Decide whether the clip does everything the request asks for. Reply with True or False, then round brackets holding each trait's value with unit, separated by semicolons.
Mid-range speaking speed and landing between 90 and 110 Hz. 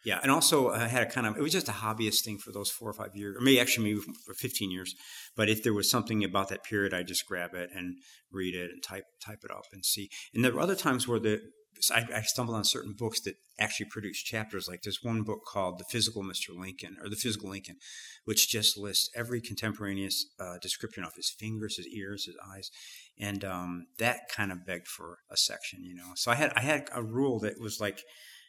False (240 wpm; 105 Hz)